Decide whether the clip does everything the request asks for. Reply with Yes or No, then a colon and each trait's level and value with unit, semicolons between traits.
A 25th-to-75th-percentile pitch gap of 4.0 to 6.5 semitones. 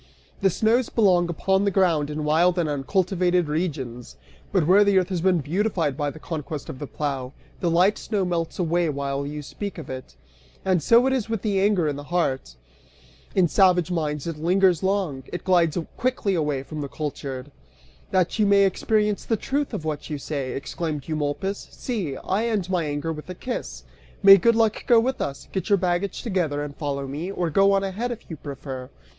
Yes: average, 4.9 semitones